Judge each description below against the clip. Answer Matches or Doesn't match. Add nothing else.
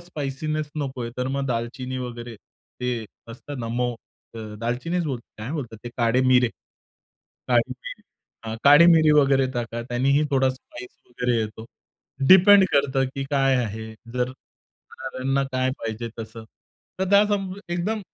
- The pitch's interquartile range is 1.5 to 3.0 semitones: Doesn't match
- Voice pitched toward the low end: Matches